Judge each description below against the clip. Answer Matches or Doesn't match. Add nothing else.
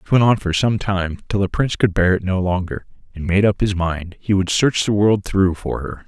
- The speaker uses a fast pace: Matches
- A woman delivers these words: Doesn't match